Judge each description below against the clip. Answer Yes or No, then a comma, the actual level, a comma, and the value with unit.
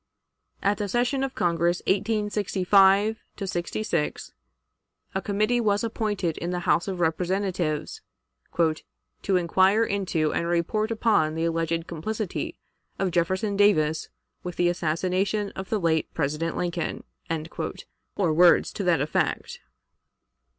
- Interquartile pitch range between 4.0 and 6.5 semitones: No, average, 3.5 semitones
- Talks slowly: Yes, slow, 120 wpm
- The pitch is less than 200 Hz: Yes, medium, 185 Hz